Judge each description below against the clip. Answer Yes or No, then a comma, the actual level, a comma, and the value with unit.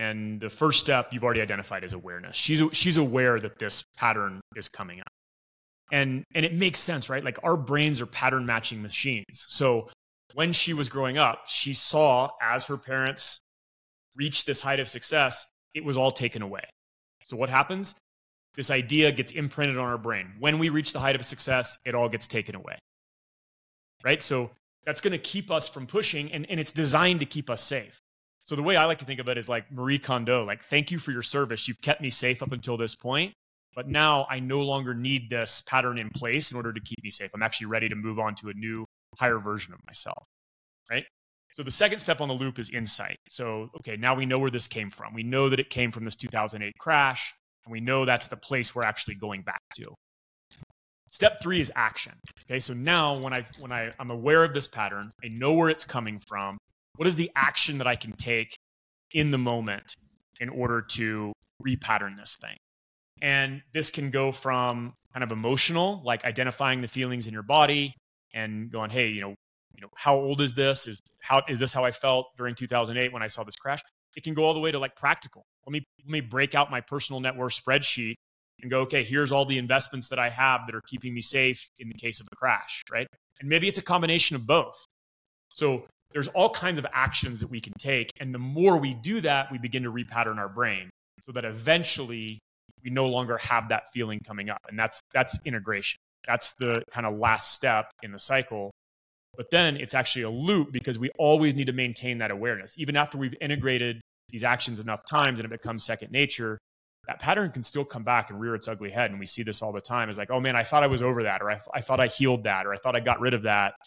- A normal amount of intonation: Yes, average, 3.9 semitones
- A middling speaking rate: No, fast, 225 wpm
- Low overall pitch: Yes, low, 125 Hz